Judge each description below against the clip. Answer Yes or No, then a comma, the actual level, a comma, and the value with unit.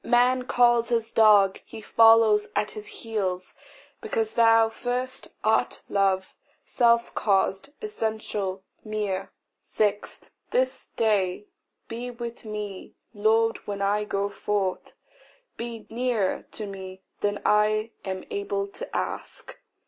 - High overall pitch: Yes, high, 215 Hz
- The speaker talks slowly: Yes, slow, 120 wpm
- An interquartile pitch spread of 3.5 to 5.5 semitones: No, narrow, 2.6 semitones